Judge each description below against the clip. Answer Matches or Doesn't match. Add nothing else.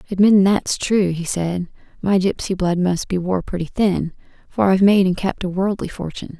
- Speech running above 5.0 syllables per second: Matches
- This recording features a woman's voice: Matches